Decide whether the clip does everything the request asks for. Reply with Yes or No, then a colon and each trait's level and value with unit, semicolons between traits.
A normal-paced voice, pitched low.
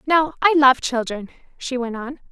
No: average, 180 wpm; very high, 265 Hz